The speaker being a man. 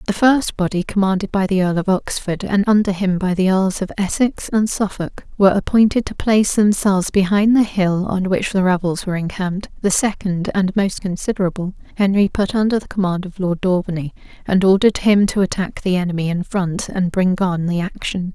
No: female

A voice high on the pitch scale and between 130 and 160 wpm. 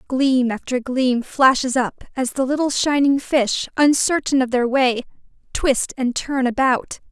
Yes: very high, 260 Hz; average, 150 wpm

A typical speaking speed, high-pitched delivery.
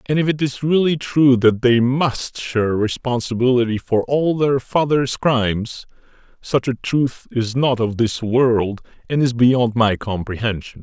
No: average, 160 wpm; low, 125 Hz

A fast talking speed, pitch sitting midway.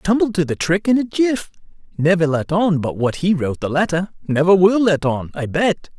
Yes: fast, 220 wpm; medium, 175 Hz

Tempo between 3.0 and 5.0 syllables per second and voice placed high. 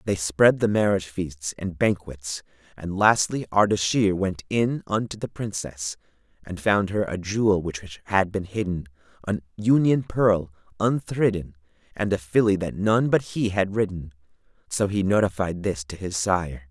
No: 4.5 syllables/s; very low, 95 Hz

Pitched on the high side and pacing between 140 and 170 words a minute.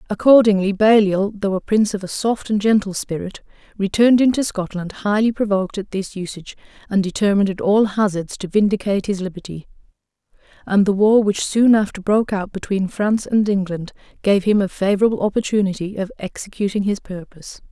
Yes: high, 200 Hz; average, 165 wpm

